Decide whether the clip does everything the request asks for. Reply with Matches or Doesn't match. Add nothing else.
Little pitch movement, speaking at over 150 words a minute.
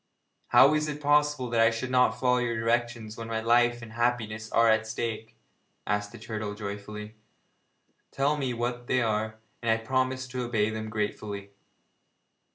Matches